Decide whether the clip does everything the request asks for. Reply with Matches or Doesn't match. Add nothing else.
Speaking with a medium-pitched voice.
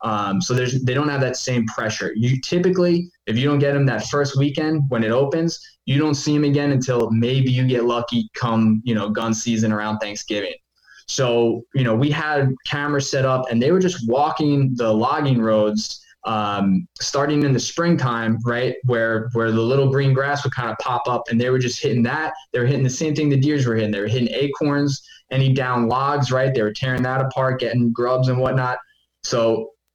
Doesn't match